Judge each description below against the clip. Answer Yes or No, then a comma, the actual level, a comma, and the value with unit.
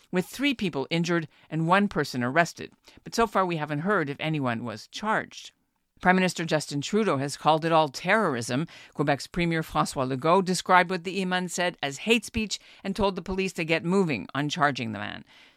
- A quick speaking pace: No, average, 195 wpm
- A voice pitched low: No, medium, 165 Hz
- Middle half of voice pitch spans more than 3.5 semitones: Yes, average, 4.6 semitones